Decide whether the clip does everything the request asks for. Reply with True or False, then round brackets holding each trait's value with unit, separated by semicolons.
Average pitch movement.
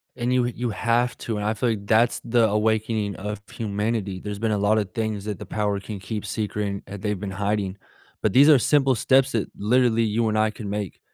False (2.2 semitones)